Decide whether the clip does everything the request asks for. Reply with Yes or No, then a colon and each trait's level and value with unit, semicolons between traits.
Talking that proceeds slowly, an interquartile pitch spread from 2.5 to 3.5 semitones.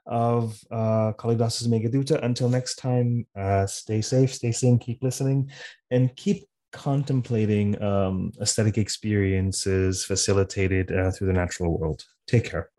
No: slow, 130 wpm; average, 4.1 semitones